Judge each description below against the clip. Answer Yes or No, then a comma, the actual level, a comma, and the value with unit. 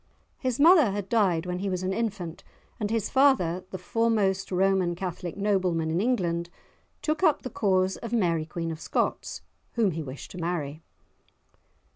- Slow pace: No, average, 165 wpm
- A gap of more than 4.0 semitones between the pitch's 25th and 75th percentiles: Yes, average, 4.5 semitones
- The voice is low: No, high, 190 Hz